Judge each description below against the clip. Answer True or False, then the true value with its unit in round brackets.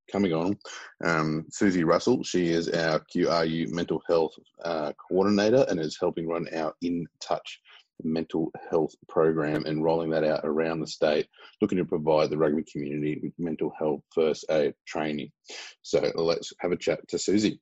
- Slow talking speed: False (165 wpm)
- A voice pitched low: True (80 Hz)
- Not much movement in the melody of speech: True (1.4 semitones)